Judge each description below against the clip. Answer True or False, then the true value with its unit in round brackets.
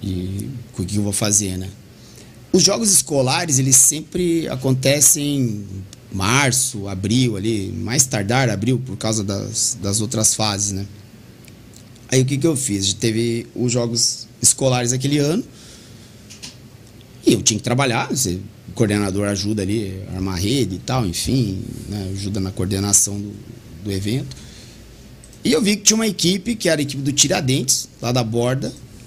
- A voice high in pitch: False (115 Hz)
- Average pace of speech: True (155 wpm)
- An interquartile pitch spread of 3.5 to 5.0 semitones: True (4.2 semitones)